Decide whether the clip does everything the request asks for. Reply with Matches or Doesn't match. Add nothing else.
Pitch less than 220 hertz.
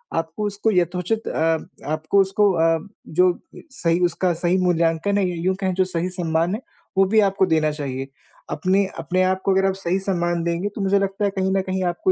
Matches